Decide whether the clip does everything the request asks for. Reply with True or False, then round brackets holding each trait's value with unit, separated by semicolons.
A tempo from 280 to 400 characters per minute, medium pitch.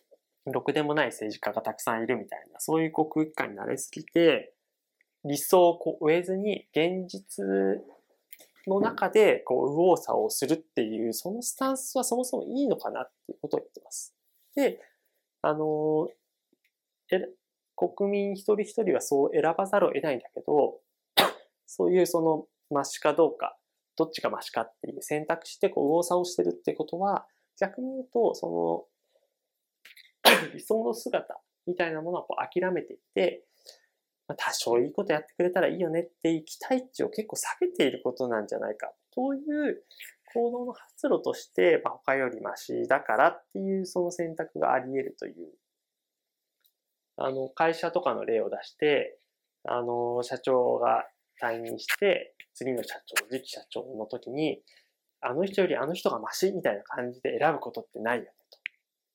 True (320 characters per minute; 180 Hz)